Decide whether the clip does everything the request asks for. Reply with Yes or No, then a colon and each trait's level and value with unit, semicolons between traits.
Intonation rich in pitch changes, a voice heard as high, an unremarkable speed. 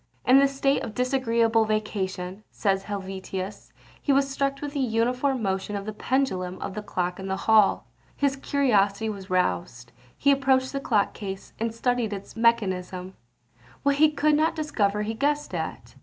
Yes: wide, 5.9 semitones; high, 220 Hz; average, 170 wpm